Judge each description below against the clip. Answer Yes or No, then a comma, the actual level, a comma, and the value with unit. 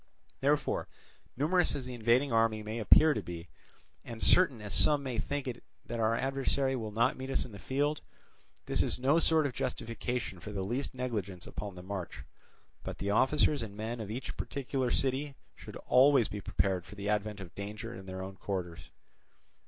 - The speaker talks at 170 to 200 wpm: Yes, average, 190 wpm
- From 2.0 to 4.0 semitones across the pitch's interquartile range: No, average, 4.8 semitones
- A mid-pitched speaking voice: No, low, 115 Hz